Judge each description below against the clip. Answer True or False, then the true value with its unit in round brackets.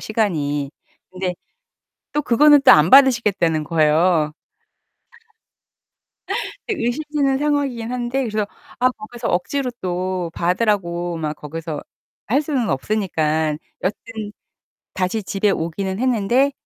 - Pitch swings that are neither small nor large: False (6.7 semitones)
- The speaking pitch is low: False (200 Hz)